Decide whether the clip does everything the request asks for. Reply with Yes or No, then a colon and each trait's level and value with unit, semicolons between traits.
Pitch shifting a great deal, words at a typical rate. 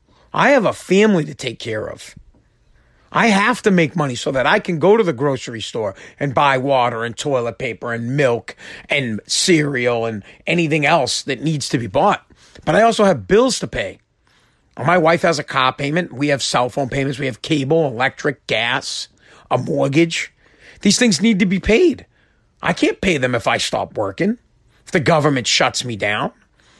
Yes: wide, 6.4 semitones; average, 190 wpm